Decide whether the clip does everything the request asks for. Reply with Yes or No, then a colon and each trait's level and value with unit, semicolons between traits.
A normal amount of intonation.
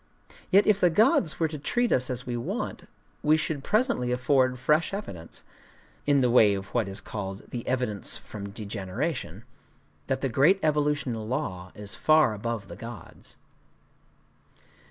No: wide, 6.3 semitones